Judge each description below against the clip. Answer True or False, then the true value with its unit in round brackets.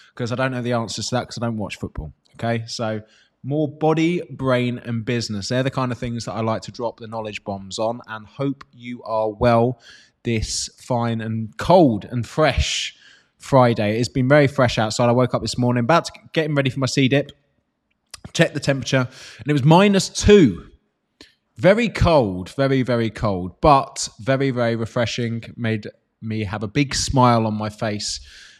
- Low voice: True (120 Hz)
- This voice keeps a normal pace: True (185 wpm)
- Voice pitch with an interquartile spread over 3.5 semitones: False (2.9 semitones)